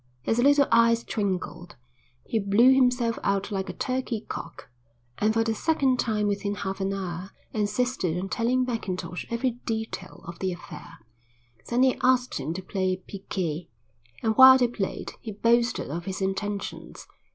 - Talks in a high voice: Yes, high, 210 Hz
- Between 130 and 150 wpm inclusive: No, average, 160 wpm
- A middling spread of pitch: Yes, average, 4.2 semitones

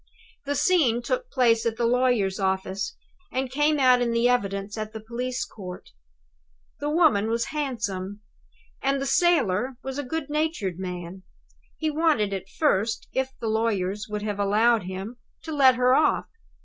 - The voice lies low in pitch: No, high, 235 Hz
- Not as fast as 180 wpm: Yes, average, 160 wpm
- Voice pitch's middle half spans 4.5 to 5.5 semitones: Yes, average, 5.1 semitones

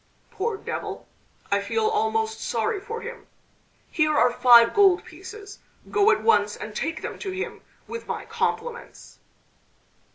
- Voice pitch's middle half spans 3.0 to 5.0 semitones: No, wide, 5.4 semitones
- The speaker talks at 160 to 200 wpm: No, average, 140 wpm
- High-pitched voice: Yes, very high, 410 Hz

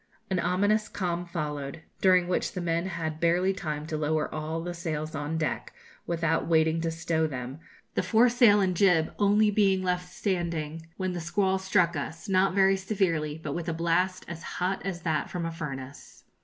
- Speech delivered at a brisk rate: No, average, 180 wpm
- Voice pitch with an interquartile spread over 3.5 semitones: No, average, 2.9 semitones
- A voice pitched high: No, medium, 170 Hz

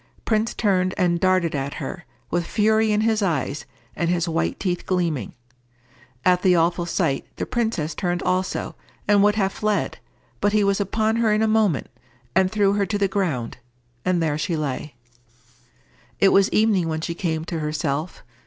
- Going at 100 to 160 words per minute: No, average, 175 wpm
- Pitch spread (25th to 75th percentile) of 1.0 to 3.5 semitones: No, average, 4.0 semitones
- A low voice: No, medium, 185 Hz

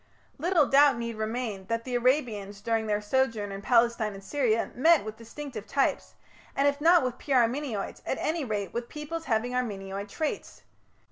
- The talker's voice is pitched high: Yes, high, 235 Hz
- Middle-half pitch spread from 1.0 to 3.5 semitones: No, average, 4.7 semitones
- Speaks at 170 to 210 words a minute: Yes, average, 175 wpm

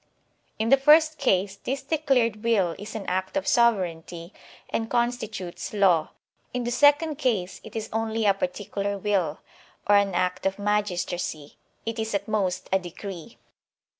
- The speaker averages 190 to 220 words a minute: No, average, 160 wpm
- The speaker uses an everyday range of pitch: Yes, average, 4.1 semitones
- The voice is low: No, high, 210 Hz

